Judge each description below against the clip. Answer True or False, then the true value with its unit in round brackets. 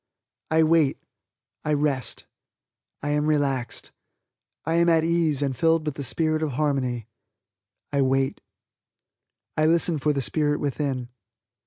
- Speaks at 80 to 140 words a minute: True (135 wpm)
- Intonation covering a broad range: False (2.7 semitones)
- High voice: False (150 Hz)